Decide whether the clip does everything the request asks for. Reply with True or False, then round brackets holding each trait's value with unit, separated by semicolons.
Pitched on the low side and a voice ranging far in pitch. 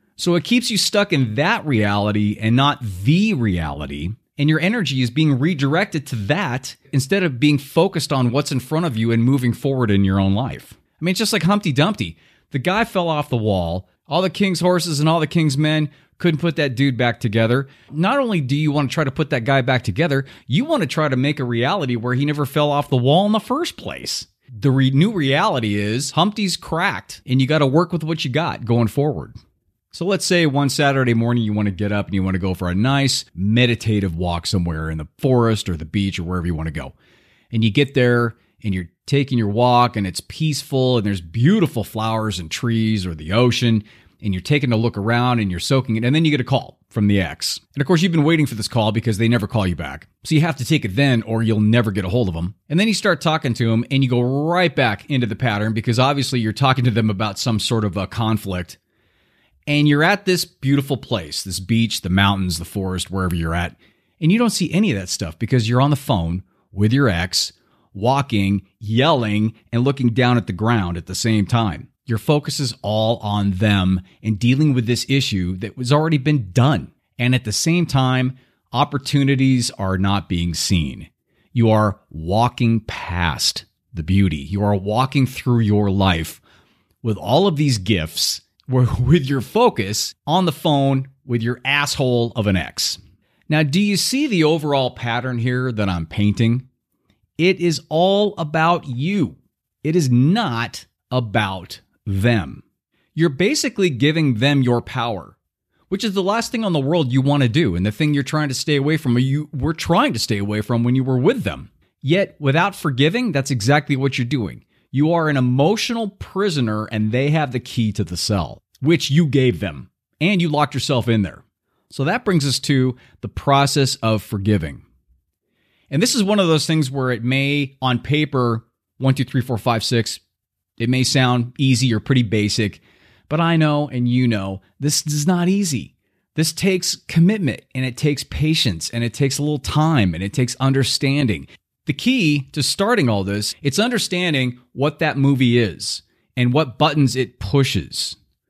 True (125 Hz; 5.7 semitones)